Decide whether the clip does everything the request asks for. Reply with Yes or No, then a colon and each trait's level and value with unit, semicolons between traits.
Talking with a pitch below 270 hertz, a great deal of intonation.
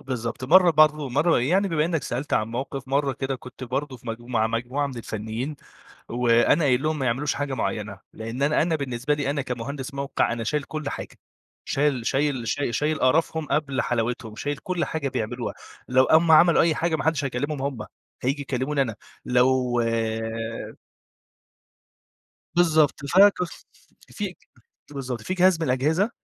No: medium, 140 Hz; average, 3.6 semitones